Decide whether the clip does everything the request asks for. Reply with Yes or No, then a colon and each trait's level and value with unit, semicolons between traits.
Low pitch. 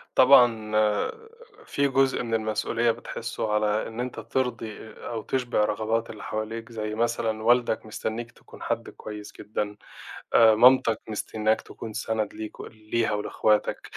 Yes: low, 110 Hz